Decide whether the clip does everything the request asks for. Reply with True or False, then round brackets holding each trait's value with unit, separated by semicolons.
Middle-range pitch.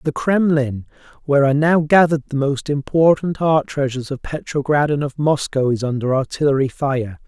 True (145 Hz)